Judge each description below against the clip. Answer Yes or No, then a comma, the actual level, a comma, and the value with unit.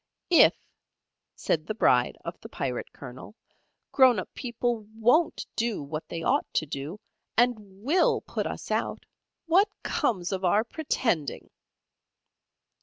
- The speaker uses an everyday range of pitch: No, wide, 7.5 semitones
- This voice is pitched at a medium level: No, high, 215 Hz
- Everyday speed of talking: No, slow, 130 wpm